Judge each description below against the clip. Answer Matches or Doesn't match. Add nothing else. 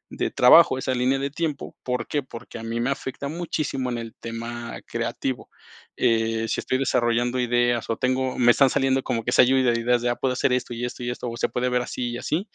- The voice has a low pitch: Matches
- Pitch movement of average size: Doesn't match